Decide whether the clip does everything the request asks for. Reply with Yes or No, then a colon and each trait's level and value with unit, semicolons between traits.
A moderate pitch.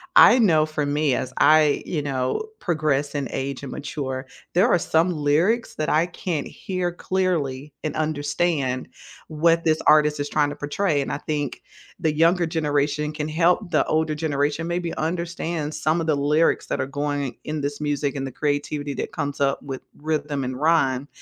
Yes: medium, 150 Hz